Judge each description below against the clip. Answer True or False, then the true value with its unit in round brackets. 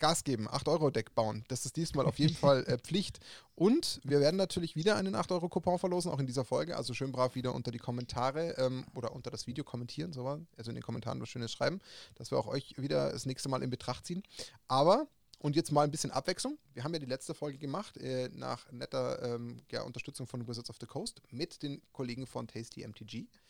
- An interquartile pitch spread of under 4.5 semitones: False (4.8 semitones)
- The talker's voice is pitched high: False (135 Hz)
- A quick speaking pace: True (230 wpm)